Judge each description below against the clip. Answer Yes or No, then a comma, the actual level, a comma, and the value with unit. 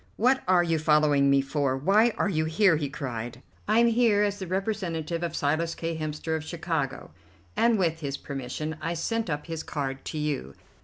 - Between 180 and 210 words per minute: Yes, average, 195 wpm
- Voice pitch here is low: No, medium, 160 Hz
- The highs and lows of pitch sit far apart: No, average, 4.5 semitones